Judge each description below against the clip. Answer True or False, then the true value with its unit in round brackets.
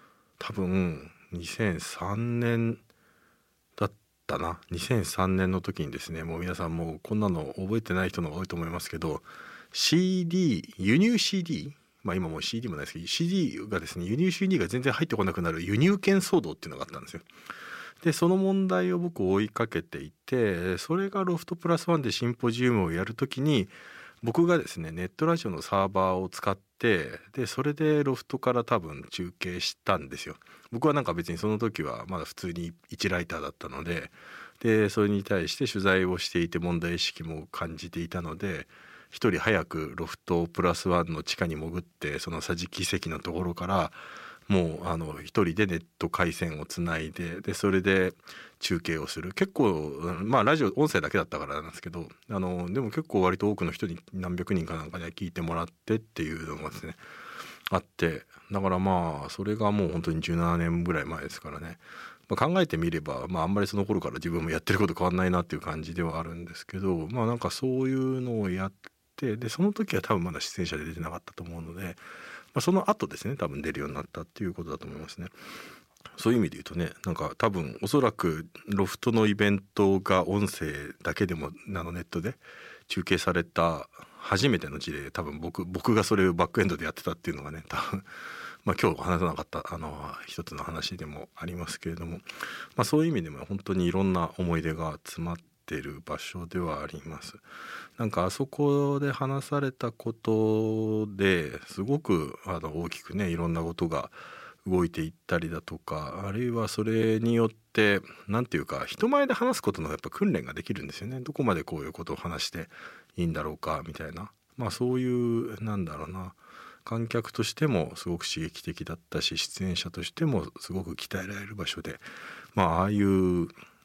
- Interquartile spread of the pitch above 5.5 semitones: False (5.2 semitones)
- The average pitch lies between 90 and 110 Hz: True (95 Hz)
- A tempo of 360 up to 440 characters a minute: True (370 characters per minute)